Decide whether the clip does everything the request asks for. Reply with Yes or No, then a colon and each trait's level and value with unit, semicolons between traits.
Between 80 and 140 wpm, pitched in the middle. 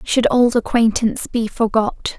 No: slow, 135 wpm; high, 230 Hz